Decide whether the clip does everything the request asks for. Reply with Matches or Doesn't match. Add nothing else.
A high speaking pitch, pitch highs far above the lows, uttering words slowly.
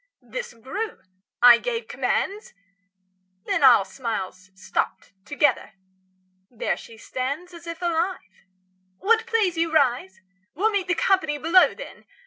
Matches